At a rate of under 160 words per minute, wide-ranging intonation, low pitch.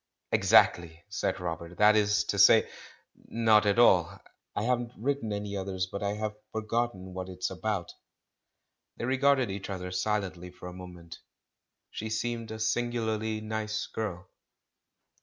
No: average, 150 wpm; average, 3.1 semitones; low, 105 Hz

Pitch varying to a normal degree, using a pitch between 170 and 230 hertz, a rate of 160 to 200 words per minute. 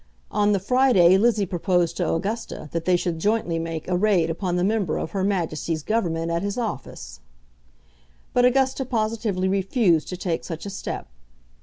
Yes: average, 4.3 semitones; high, 190 Hz; average, 170 wpm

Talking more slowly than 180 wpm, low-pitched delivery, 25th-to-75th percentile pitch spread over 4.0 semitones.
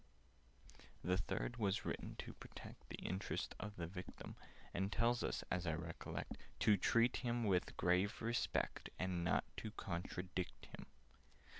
No: average, 150 wpm; very low, 95 Hz; average, 3.7 semitones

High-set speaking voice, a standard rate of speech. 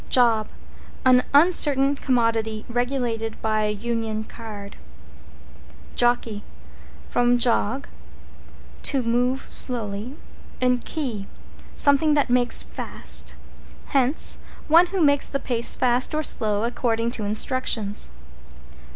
No: high, 245 Hz; slow, 105 wpm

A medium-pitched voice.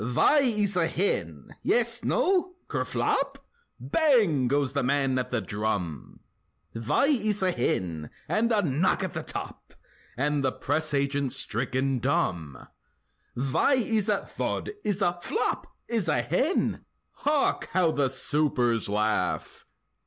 Yes: medium, 145 Hz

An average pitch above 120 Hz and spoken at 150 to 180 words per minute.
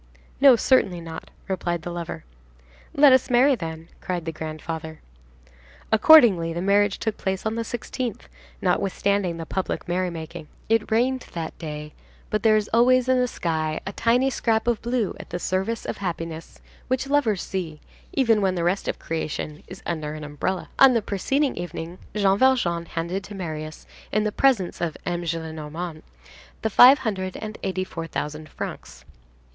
Yes: medium, 185 Hz; average, 165 wpm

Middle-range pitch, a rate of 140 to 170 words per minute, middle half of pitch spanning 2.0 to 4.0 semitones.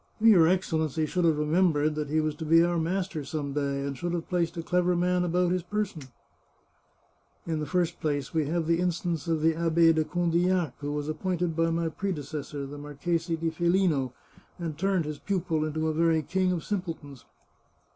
No: medium, 165 Hz; average, 200 wpm; narrow, 2.5 semitones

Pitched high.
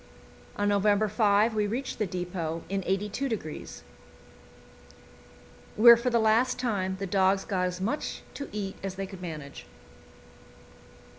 Yes: high, 200 Hz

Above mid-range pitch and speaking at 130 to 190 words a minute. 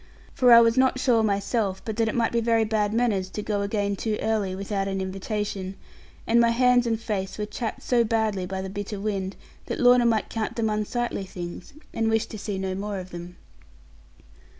No: high, 215 Hz; fast, 205 wpm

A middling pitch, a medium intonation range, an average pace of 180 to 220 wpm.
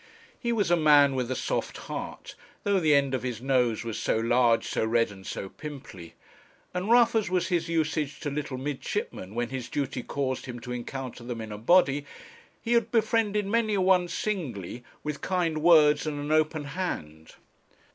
No: medium, 145 Hz; wide, 6.6 semitones; average, 185 wpm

